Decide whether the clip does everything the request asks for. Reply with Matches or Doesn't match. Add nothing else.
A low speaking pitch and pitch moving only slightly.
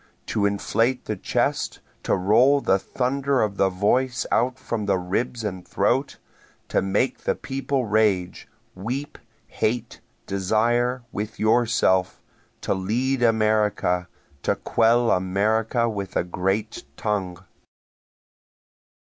Doesn't match